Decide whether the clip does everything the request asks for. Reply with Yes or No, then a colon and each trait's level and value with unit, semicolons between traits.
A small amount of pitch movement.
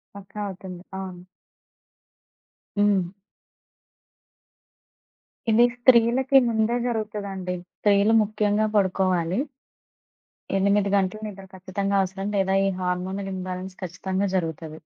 Yes: narrow, 2.2 semitones